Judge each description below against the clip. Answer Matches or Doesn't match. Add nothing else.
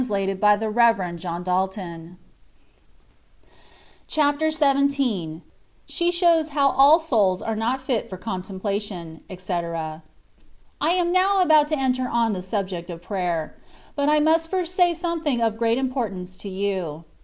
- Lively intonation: Matches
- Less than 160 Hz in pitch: Doesn't match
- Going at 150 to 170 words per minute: Doesn't match